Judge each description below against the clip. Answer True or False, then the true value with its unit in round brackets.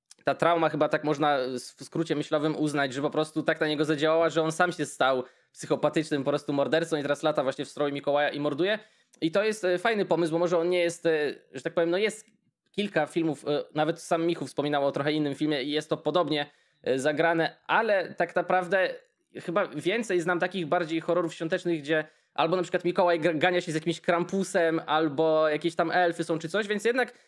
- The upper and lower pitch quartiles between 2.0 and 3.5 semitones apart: True (2.7 semitones)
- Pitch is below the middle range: False (165 Hz)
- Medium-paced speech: False (205 wpm)